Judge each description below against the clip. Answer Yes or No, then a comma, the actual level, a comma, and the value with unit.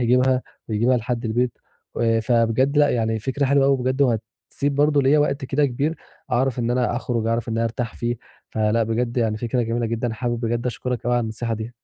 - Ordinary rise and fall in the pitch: No, narrow, 2.2 semitones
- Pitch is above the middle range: No, low, 120 Hz